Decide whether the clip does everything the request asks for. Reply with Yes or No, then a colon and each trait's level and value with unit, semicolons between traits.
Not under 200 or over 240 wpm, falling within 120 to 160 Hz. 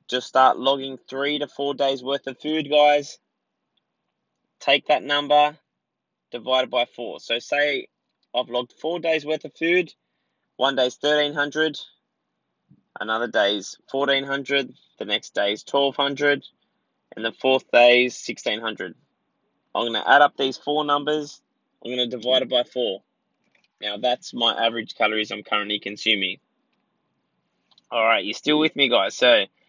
No: average, 150 wpm; medium, 140 Hz